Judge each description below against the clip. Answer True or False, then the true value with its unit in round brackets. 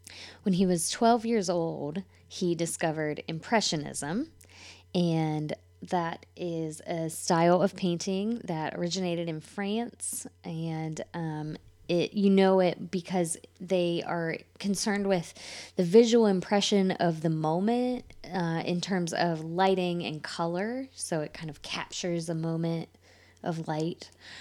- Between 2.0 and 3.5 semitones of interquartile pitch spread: True (3.0 semitones)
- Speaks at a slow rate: True (130 wpm)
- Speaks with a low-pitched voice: False (175 Hz)